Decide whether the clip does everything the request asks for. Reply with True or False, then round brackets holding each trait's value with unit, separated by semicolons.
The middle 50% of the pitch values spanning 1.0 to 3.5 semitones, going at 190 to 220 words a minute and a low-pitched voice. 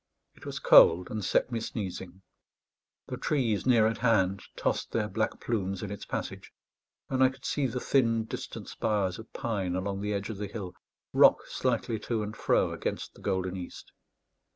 False (3.1 semitones; 180 wpm; 105 Hz)